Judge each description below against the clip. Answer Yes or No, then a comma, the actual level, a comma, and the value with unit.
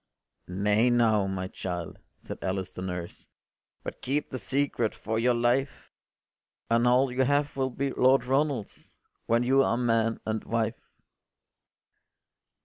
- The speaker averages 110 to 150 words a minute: Yes, average, 140 wpm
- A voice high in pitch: No, low, 120 Hz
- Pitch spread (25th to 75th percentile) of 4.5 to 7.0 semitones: No, average, 3.8 semitones